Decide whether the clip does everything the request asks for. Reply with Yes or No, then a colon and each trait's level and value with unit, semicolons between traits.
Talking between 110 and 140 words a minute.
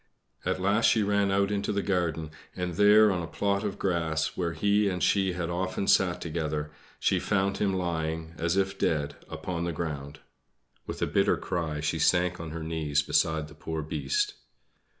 No: average, 185 wpm